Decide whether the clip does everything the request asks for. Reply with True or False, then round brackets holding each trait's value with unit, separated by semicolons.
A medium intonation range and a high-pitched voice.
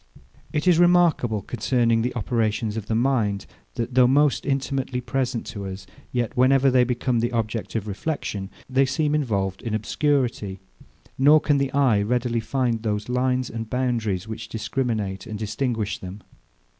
False (3.6 semitones; 120 Hz)